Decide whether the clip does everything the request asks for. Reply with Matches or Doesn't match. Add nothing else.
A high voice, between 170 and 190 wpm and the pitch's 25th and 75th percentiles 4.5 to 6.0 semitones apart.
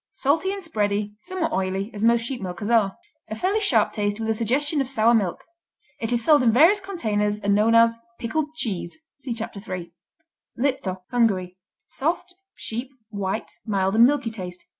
Matches